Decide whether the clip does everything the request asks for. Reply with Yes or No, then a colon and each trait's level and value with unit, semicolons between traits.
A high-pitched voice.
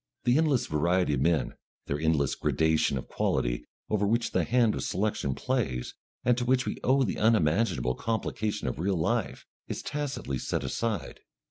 No: low, 100 Hz